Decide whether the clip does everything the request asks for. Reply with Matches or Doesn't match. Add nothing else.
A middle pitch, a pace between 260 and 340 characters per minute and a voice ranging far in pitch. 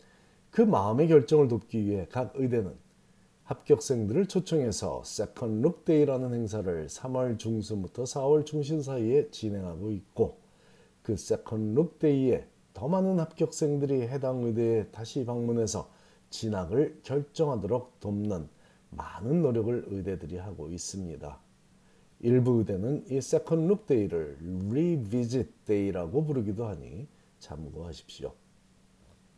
Doesn't match